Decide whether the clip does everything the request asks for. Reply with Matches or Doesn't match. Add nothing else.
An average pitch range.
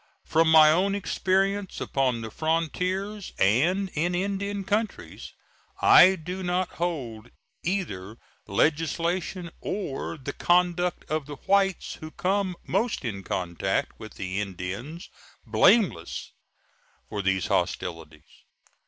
Doesn't match